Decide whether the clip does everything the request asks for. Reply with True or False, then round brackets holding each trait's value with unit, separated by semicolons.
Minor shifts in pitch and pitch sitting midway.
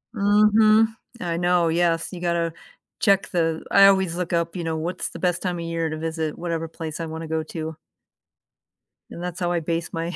True (1.7 semitones; 170 Hz)